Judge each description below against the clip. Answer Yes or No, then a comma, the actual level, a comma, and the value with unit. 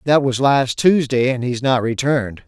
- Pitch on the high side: No, low, 130 Hz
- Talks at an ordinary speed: No, fast, 220 wpm